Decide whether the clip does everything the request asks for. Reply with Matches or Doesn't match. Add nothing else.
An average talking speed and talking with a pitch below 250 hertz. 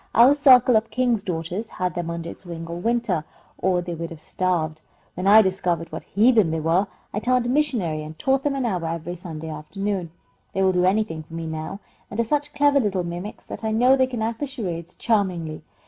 Doesn't match